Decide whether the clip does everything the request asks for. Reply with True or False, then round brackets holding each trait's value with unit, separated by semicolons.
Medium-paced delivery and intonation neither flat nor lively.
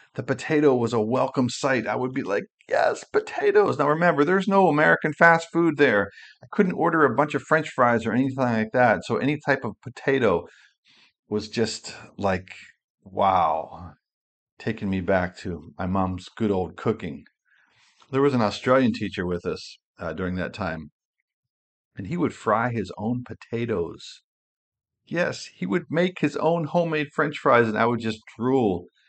False (170 wpm; 6.2 semitones)